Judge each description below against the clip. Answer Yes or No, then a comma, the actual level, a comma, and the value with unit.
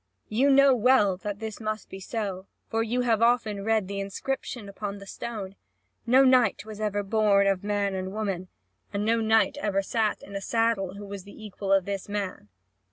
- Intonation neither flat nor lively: No, narrow, 2.2 semitones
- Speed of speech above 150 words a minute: Yes, average, 195 wpm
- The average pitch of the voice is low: No, high, 205 Hz